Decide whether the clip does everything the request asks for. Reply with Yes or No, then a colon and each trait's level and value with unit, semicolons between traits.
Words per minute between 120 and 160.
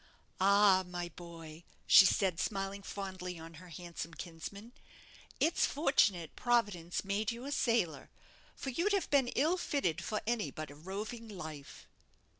Yes: average, 145 wpm